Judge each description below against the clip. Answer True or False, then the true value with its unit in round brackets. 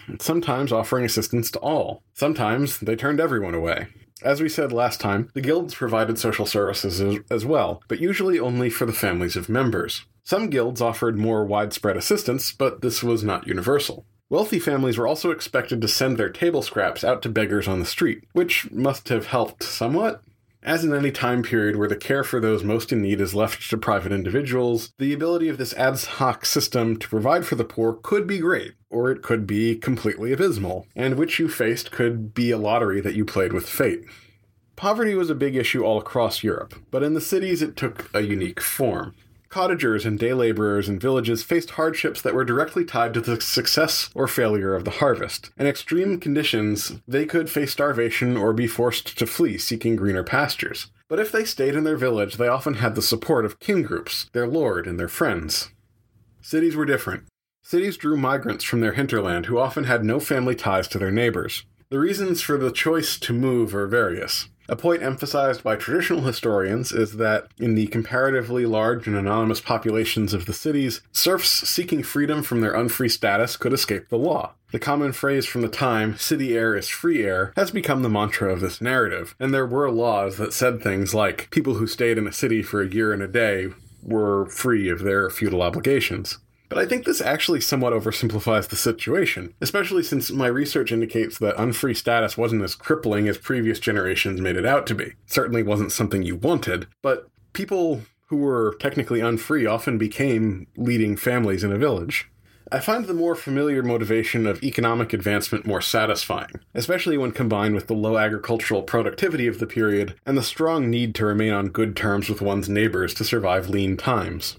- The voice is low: True (115 Hz)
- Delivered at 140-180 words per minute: False (195 wpm)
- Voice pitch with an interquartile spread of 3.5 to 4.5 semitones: True (4.2 semitones)